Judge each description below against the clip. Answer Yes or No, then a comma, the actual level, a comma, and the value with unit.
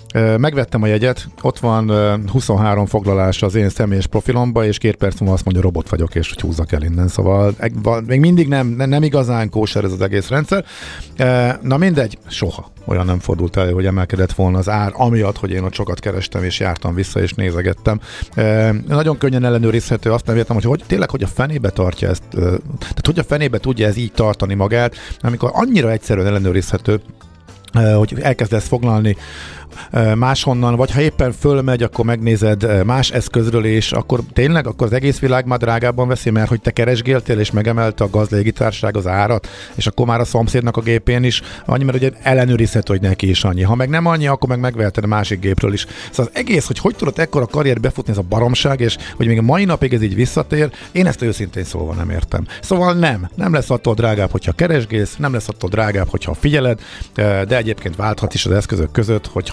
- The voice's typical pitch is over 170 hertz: No, low, 110 Hz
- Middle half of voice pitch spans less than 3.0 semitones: No, average, 4.2 semitones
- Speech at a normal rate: No, fast, 195 wpm